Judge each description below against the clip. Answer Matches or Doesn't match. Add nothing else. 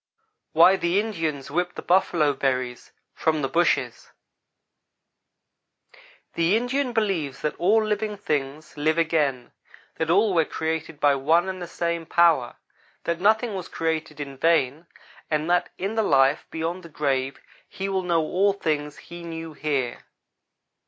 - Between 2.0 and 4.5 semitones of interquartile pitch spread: Matches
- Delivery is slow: Doesn't match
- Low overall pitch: Doesn't match